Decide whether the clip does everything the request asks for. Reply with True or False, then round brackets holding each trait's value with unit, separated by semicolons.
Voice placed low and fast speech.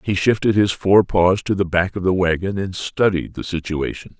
True (95 Hz; 215 wpm)